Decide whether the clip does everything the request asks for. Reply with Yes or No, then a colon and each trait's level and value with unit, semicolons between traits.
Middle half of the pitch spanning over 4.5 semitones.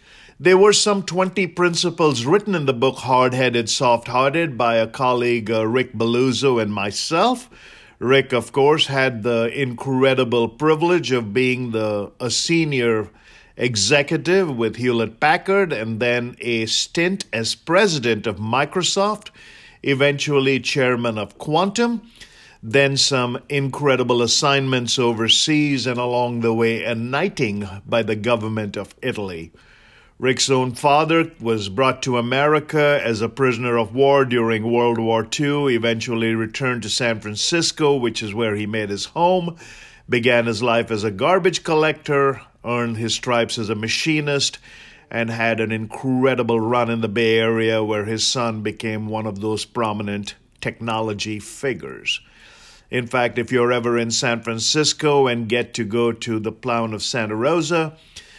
No: average, 3.8 semitones